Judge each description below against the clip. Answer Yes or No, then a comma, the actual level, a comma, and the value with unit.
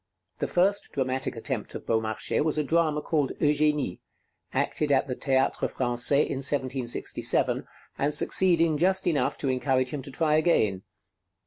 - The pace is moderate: Yes, average, 145 wpm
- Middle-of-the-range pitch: Yes, medium, 145 Hz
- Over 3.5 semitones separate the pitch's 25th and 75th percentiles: No, average, 3.1 semitones